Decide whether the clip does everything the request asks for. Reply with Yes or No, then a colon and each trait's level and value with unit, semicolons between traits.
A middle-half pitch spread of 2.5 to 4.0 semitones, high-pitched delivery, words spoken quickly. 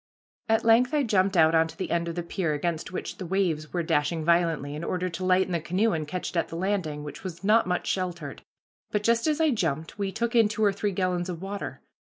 No: average, 3.6 semitones; medium, 180 Hz; fast, 245 wpm